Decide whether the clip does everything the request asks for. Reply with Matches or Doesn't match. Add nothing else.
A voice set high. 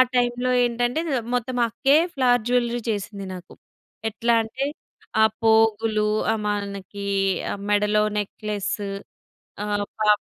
Matches